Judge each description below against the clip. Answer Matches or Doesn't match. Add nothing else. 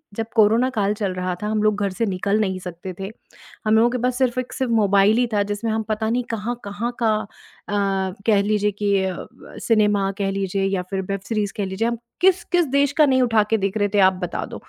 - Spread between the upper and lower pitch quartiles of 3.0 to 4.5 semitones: Doesn't match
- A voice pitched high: Matches